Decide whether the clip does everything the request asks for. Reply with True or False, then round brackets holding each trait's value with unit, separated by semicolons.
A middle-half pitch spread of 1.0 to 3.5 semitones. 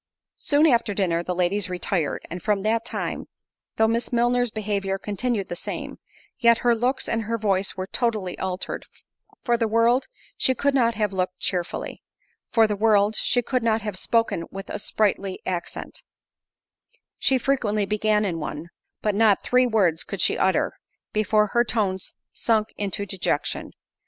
True (3.2 semitones)